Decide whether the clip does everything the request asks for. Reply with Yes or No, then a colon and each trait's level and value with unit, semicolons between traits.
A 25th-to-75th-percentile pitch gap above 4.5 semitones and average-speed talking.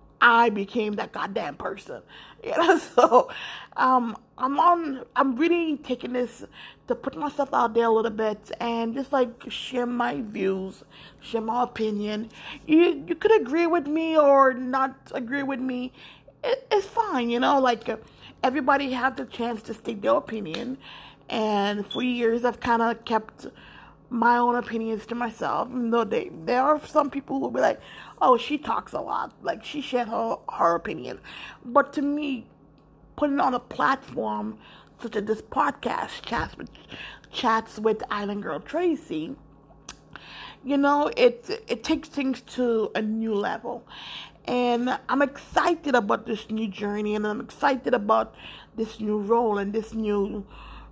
No: average, 4.1 semitones; average, 160 wpm